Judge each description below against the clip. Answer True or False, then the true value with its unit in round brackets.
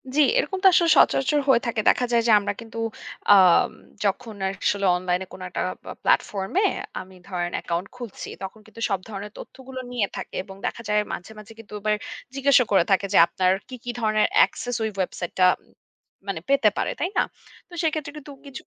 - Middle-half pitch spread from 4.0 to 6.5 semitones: True (4.7 semitones)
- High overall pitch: True (215 Hz)